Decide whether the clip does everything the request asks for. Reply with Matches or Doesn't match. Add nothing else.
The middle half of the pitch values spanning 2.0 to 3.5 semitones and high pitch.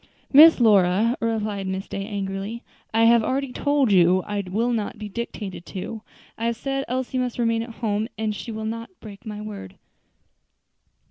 Matches